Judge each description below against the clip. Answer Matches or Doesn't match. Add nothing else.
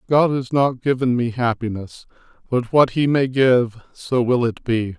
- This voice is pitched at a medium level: Doesn't match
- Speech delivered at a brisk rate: Doesn't match